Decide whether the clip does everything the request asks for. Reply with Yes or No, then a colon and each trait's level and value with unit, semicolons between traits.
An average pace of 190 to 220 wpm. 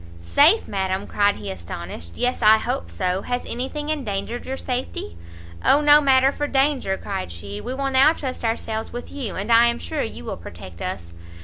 Yes: average, 195 wpm